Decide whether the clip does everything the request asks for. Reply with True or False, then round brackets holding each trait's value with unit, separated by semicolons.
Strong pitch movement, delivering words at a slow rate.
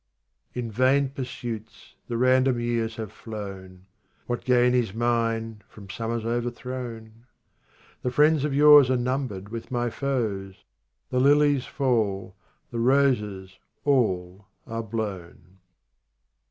False (3.4 semitones; 120 wpm)